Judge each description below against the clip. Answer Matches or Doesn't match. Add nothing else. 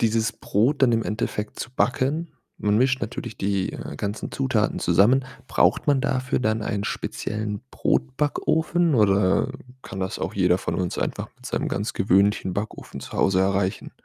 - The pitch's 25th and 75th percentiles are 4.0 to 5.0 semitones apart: Matches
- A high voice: Doesn't match